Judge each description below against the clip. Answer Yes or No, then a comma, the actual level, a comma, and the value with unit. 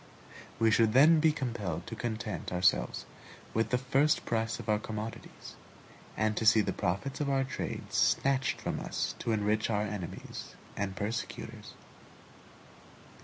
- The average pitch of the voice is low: Yes, low, 110 Hz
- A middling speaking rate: Yes, average, 145 wpm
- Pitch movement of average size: Yes, average, 3.9 semitones